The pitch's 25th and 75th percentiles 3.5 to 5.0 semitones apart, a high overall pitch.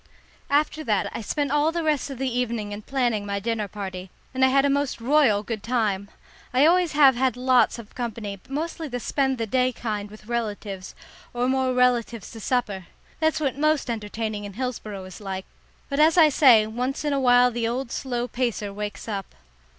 Yes: average, 4.3 semitones; high, 245 Hz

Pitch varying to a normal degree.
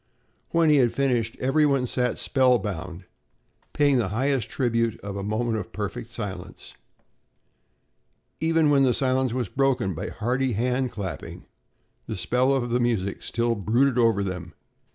Yes: average, 4.2 semitones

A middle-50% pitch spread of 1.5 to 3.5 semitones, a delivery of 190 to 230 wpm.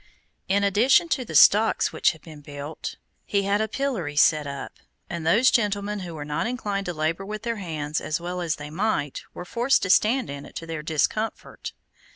No: wide, 5.6 semitones; average, 200 wpm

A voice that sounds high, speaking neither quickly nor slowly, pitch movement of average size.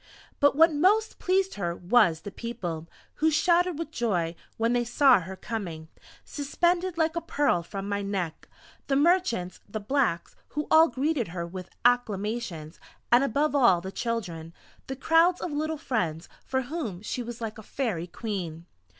No: high, 235 Hz; average, 165 wpm; wide, 8.6 semitones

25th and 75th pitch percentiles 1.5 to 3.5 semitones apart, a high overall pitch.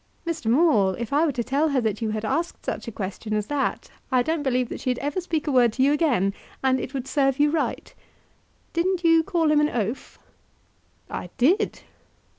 No: average, 5.0 semitones; very high, 275 Hz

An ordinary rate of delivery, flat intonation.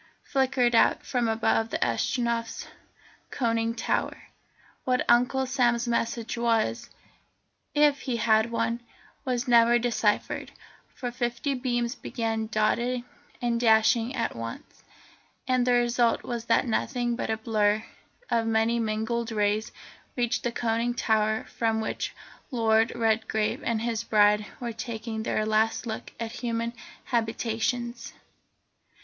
No: slow, 125 wpm; narrow, 1.4 semitones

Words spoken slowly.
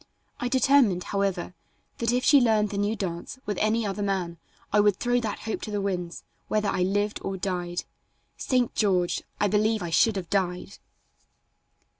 No: average, 175 wpm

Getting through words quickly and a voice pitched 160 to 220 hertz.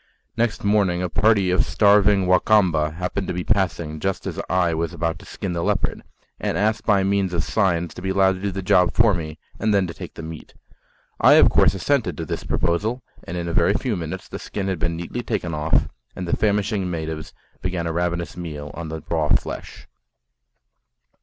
No: fast, 210 wpm; very low, 90 Hz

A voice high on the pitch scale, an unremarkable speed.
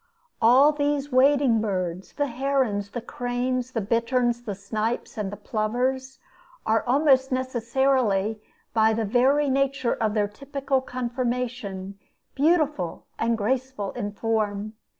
No: high, 245 Hz; slow, 125 wpm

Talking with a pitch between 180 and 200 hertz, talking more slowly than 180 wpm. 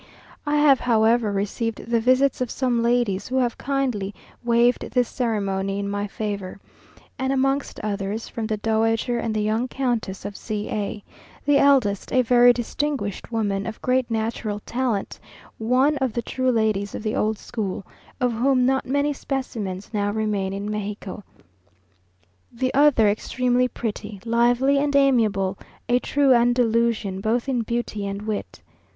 No: high, 230 Hz; average, 155 wpm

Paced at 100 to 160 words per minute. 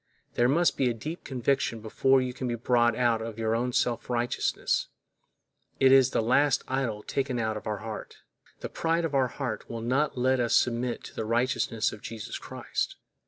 No: average, 190 wpm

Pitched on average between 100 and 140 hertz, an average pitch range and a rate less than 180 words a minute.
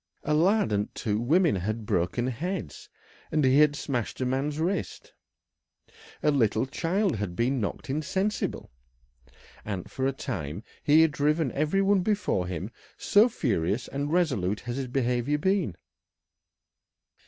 No: low, 135 Hz; wide, 6.6 semitones; average, 140 wpm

